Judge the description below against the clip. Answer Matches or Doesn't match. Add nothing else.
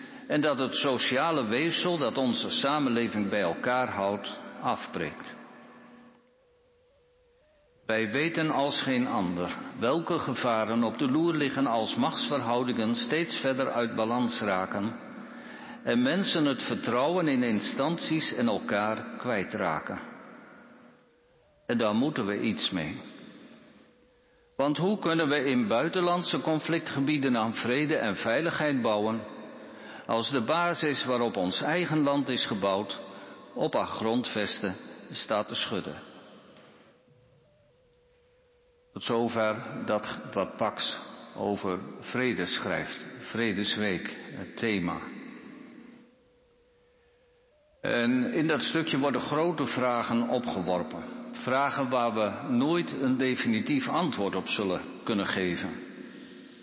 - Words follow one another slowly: Matches